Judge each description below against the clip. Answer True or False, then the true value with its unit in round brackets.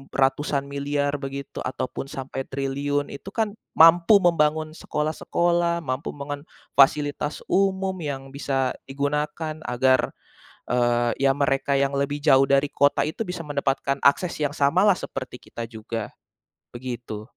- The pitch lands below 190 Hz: True (140 Hz)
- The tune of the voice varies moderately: False (2.3 semitones)